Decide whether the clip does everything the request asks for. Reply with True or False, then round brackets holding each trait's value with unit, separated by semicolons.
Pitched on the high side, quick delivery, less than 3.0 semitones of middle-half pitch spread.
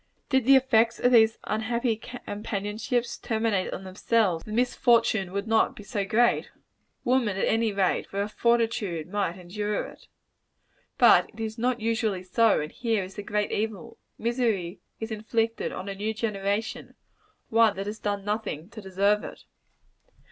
False (215 Hz; 160 wpm; 2.5 semitones)